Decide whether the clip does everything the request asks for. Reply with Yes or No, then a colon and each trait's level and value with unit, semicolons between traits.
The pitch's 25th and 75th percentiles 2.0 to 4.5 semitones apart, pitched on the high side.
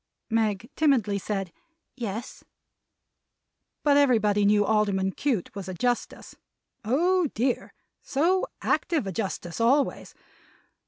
No: wide, 5.6 semitones; high, 225 Hz